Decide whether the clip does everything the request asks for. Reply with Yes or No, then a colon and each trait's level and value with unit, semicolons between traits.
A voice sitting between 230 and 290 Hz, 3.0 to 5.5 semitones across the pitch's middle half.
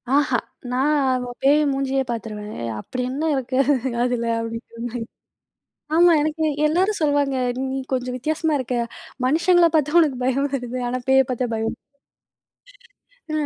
Yes: very high, 265 Hz; average, 3.4 semitones